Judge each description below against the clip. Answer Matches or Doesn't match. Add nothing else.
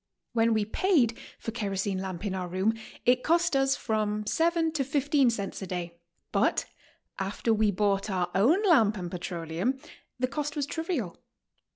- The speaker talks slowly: Doesn't match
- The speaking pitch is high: Matches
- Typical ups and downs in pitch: Doesn't match